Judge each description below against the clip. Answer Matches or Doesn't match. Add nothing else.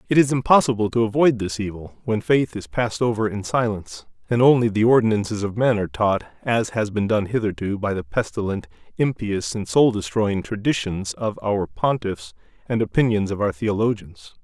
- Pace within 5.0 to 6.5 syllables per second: Matches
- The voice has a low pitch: Matches